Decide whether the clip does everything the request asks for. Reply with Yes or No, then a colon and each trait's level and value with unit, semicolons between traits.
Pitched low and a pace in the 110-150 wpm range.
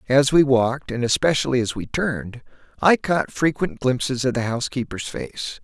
No: low, 130 Hz; average, 170 wpm